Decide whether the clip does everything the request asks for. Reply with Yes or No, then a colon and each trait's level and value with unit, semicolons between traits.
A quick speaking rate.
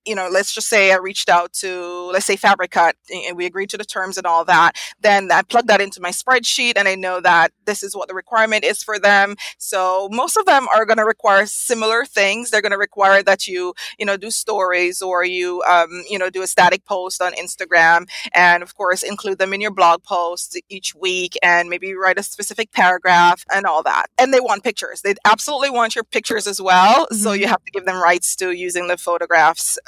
Yes: fast, 225 wpm